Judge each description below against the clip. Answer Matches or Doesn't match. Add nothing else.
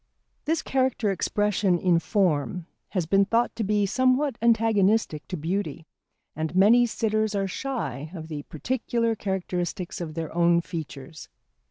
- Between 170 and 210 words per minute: Doesn't match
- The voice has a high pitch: Matches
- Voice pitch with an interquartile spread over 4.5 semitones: Matches